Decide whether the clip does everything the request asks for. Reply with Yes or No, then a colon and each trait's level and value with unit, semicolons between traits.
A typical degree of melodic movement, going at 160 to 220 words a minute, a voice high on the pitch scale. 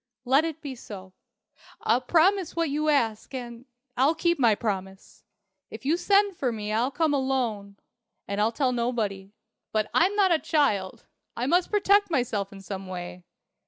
No: wide, 7.3 semitones; average, 165 wpm; very high, 250 Hz